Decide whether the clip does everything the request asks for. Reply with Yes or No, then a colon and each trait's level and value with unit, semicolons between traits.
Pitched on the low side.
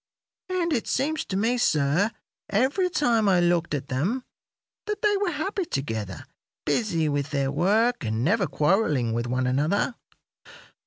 No: medium, 185 Hz